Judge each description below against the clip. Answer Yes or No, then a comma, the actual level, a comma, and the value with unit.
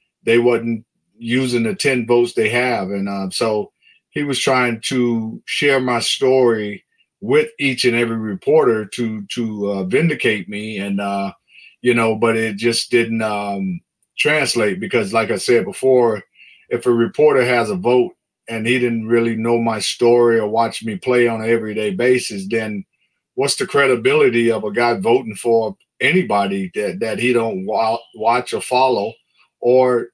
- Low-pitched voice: Yes, low, 115 Hz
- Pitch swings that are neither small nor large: No, narrow, 2.2 semitones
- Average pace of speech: Yes, average, 165 wpm